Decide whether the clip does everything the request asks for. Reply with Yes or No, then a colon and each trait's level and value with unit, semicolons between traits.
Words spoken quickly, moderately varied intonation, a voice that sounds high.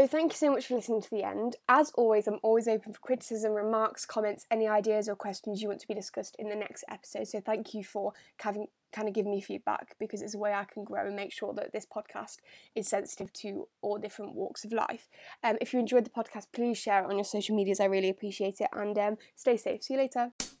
No: fast, 255 wpm; narrow, 2.0 semitones; high, 215 Hz